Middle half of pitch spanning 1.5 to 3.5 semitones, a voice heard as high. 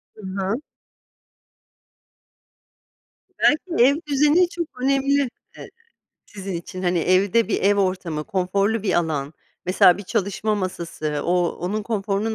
No: average, 4.2 semitones; high, 200 Hz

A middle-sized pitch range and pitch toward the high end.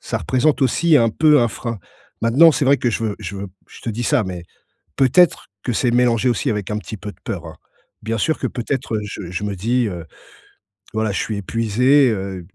No: average, 3.9 semitones; low, 115 Hz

